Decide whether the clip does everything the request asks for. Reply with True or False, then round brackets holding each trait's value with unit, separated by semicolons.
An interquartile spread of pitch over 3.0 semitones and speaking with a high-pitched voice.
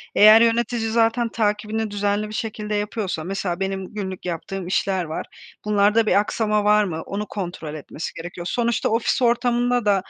False (2.7 semitones; 210 Hz)